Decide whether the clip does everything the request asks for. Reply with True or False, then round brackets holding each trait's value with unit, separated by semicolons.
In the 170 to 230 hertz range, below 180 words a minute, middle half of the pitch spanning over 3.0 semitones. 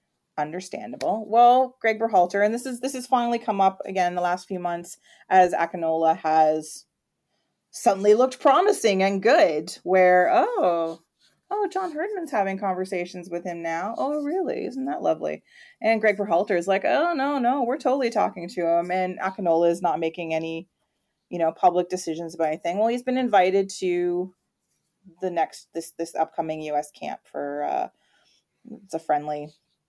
True (185 Hz; 165 wpm; 5.5 semitones)